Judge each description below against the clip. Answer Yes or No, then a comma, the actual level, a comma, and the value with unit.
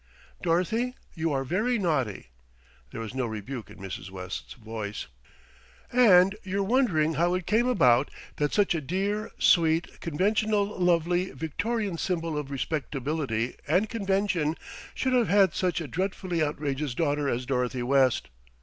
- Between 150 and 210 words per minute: No, average, 140 wpm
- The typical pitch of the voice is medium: Yes, medium, 165 Hz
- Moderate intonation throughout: No, wide, 6.4 semitones